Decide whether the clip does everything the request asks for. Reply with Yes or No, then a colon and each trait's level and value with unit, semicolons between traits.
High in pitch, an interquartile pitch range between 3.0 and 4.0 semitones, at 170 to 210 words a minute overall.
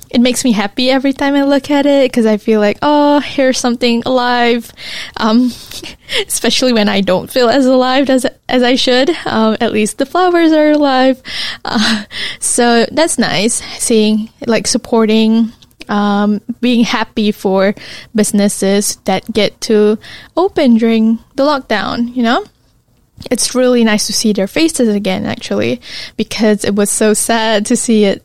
No: high, 235 Hz; average, 3.3 semitones; average, 160 wpm